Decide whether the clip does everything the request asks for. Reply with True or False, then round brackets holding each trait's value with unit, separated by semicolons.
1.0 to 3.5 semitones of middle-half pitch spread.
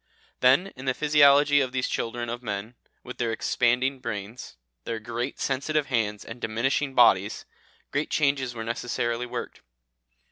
True (2.7 semitones)